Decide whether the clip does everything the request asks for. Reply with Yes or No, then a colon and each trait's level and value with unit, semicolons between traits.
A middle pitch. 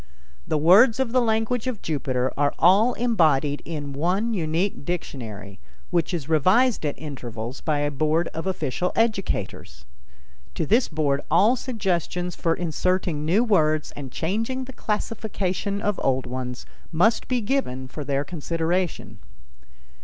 Yes: medium, 170 Hz